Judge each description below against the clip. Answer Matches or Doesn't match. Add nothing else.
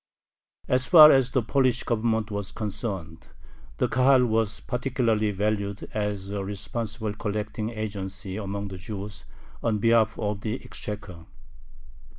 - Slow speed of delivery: Matches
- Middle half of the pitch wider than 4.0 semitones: Doesn't match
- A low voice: Matches